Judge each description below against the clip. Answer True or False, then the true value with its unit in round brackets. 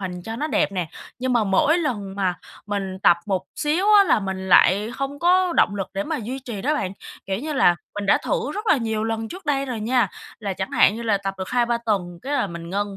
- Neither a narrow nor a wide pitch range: False (6.0 semitones)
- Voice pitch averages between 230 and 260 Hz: False (220 Hz)